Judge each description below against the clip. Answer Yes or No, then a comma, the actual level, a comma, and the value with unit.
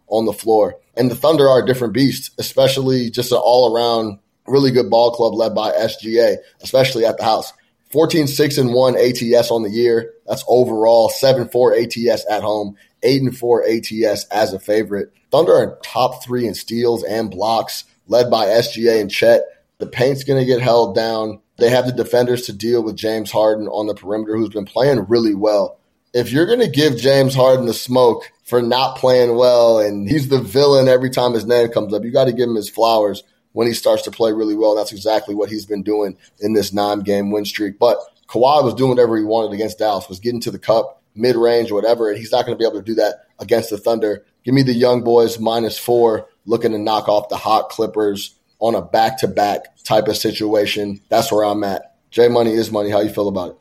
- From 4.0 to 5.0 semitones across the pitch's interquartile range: No, average, 2.7 semitones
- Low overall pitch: Yes, low, 115 Hz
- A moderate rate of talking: No, fast, 215 wpm